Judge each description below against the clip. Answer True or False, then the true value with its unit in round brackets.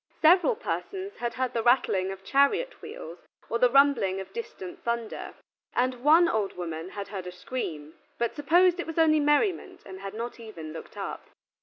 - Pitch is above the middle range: True (245 Hz)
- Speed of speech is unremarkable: True (180 wpm)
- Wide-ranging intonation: True (9.0 semitones)